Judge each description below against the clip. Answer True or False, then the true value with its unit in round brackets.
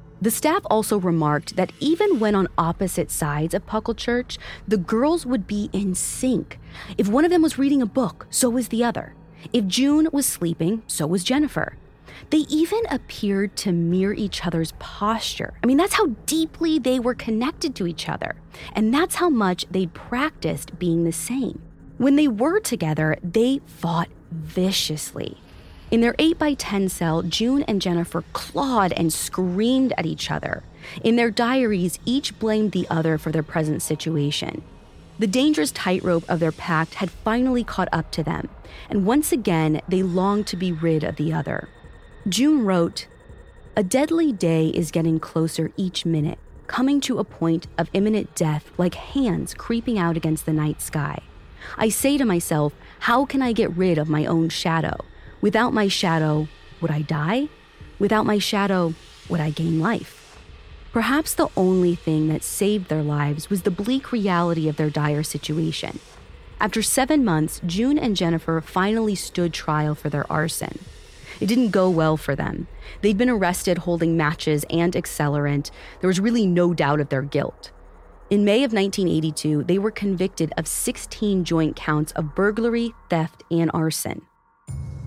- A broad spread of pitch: True (6.3 semitones)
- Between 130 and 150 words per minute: False (165 wpm)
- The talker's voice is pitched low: False (185 Hz)